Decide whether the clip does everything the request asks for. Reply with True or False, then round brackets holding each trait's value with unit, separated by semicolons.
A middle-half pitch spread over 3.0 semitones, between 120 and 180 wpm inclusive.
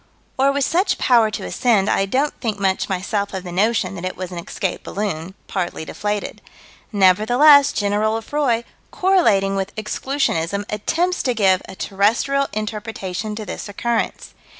True (4.0 semitones; 150 wpm)